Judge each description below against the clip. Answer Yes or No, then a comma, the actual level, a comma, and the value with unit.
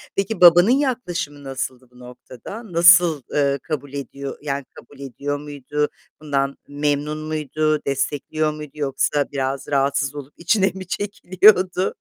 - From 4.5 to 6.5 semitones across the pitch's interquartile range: No, average, 3.7 semitones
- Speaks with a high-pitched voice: No, medium, 145 Hz